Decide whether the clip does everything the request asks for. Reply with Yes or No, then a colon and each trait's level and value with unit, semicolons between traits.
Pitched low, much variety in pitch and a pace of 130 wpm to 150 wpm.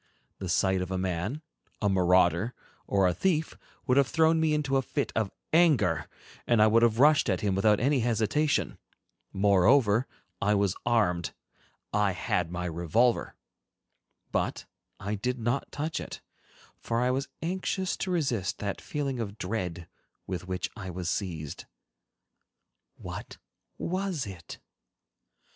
Yes: low, 110 Hz; wide, 6.7 semitones; average, 140 wpm